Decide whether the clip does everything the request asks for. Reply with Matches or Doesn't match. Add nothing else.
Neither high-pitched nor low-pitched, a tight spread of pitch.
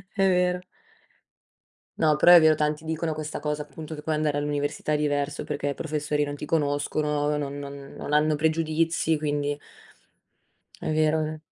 Matches